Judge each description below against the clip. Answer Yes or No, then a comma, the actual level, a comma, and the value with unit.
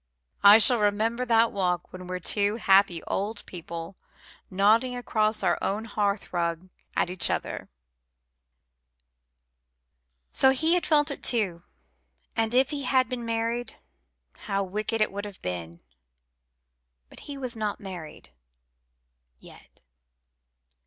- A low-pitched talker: No, high, 210 Hz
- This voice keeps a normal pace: No, slow, 125 wpm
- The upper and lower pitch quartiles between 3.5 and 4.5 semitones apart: Yes, average, 4.1 semitones